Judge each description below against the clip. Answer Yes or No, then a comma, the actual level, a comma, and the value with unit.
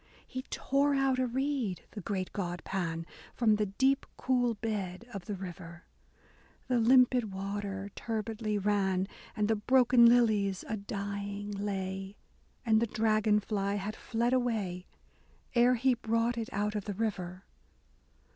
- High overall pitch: Yes, high, 210 Hz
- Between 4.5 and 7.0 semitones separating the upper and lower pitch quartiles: No, average, 3.2 semitones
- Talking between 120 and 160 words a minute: Yes, average, 145 wpm